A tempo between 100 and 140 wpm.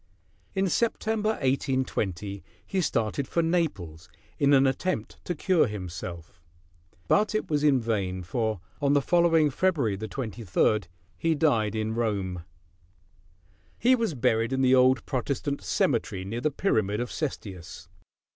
Yes: slow, 135 wpm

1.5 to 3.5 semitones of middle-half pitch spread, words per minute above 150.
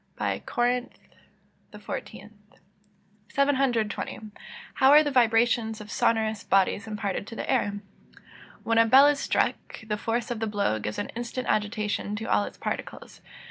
No: average, 2.8 semitones; average, 140 wpm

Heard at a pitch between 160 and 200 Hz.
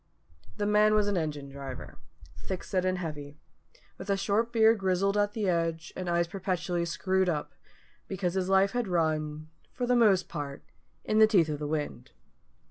Yes: medium, 185 Hz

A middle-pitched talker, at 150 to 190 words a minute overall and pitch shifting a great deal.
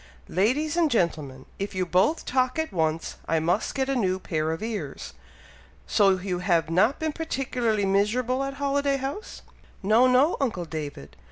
No: high, 215 Hz; average, 165 wpm; wide, 7.4 semitones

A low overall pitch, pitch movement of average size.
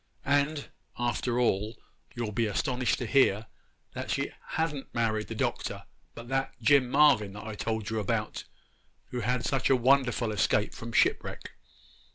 Yes: low, 120 Hz; average, 3.5 semitones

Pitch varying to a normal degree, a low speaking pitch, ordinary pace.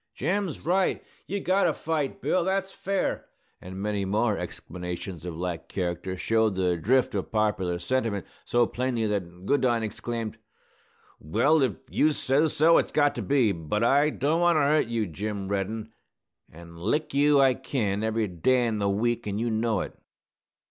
No: wide, 6.5 semitones; low, 115 Hz; average, 170 wpm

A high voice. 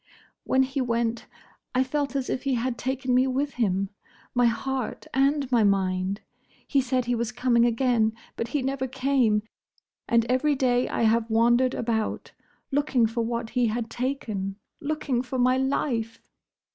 Yes: high, 245 Hz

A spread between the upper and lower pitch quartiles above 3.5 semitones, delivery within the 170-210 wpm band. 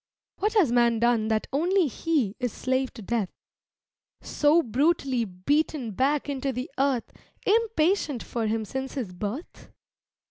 No: average, 5.0 semitones; average, 140 wpm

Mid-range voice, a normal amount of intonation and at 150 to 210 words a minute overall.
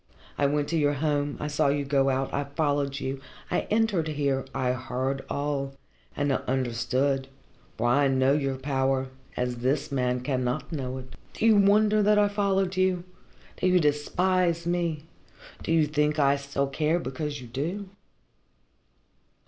Yes: medium, 145 Hz; average, 3.7 semitones; average, 165 wpm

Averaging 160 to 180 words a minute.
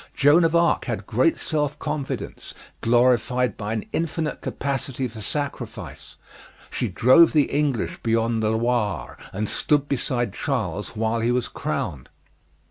No: slow, 135 wpm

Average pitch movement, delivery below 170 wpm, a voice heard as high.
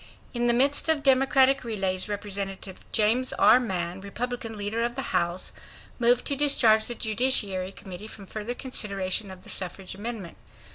Yes: average, 4.3 semitones; average, 155 wpm; high, 220 Hz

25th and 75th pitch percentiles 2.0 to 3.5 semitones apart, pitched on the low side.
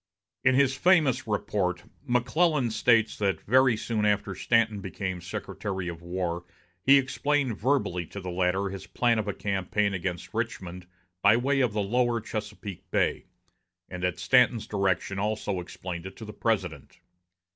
No: average, 4.6 semitones; low, 105 Hz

